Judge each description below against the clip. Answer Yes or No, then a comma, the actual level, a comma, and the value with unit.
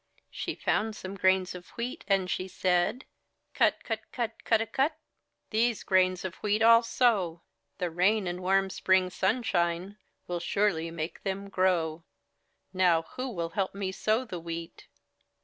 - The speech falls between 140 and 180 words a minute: Yes, average, 150 wpm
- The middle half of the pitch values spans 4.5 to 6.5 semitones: No, average, 3.5 semitones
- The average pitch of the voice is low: No, high, 190 Hz